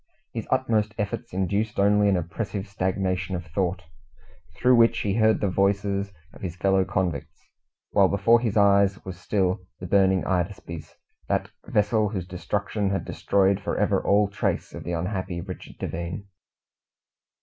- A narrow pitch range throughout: Yes, narrow, 1.9 semitones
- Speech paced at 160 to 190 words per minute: No, average, 150 wpm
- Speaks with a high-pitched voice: No, low, 100 Hz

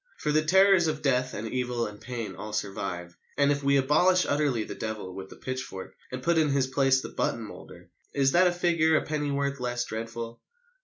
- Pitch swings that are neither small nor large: Yes, average, 4.7 semitones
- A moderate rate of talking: No, fast, 210 wpm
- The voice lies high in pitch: No, low, 135 Hz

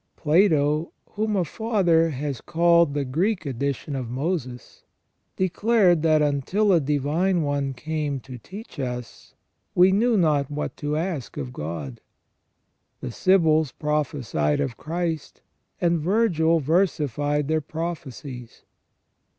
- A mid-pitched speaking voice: Yes, medium, 155 Hz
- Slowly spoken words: Yes, slow, 120 wpm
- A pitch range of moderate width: Yes, average, 3.9 semitones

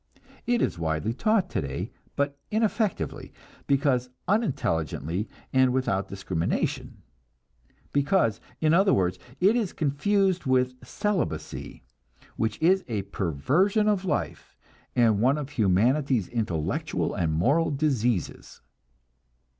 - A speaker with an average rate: No, slow, 105 wpm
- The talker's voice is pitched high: No, low, 135 Hz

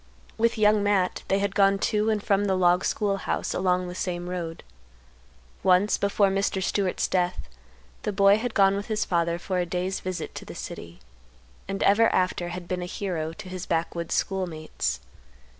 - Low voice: No, high, 190 Hz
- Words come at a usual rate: Yes, average, 180 wpm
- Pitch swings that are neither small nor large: No, narrow, 2.1 semitones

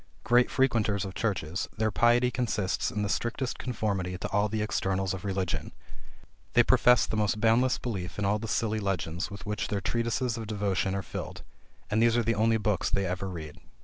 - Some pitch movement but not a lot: Yes, average, 3.0 semitones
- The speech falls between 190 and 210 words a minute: Yes, average, 195 wpm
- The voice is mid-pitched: No, low, 105 Hz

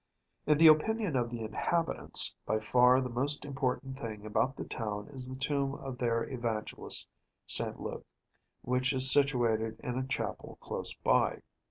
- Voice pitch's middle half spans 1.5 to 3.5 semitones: Yes, average, 3.0 semitones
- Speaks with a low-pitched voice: Yes, low, 130 Hz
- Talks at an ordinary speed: Yes, average, 160 wpm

